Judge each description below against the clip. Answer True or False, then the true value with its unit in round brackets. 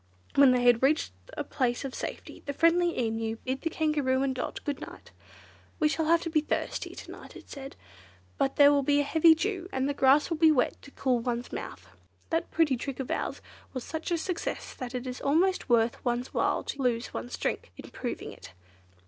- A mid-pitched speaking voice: False (275 Hz)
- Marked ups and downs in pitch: False (4.1 semitones)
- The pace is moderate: False (215 wpm)